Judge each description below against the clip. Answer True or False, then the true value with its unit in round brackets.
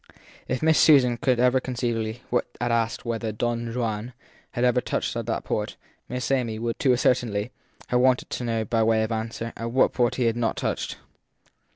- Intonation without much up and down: True (1.7 semitones)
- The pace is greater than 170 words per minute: True (190 wpm)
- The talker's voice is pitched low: True (120 Hz)